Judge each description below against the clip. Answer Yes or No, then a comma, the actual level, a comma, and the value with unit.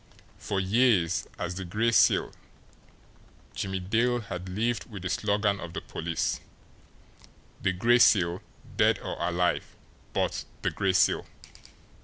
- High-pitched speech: No, very low, 95 Hz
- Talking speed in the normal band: No, slow, 130 wpm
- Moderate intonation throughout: Yes, average, 3.8 semitones